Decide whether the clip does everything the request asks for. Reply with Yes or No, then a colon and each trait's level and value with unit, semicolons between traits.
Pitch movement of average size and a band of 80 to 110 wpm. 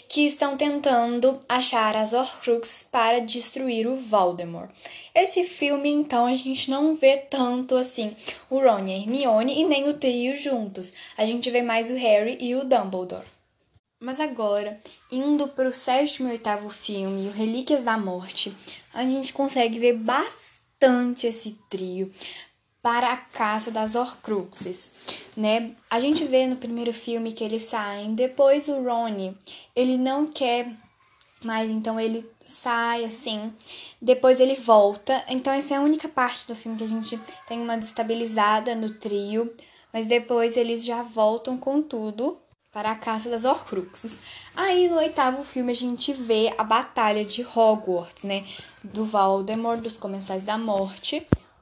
No: average, 3.0 semitones; average, 155 wpm